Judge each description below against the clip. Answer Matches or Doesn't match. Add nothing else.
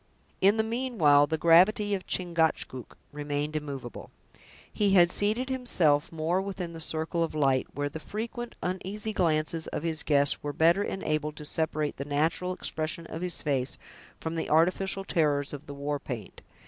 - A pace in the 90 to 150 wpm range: Doesn't match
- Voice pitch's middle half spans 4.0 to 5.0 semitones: Matches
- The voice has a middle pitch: Matches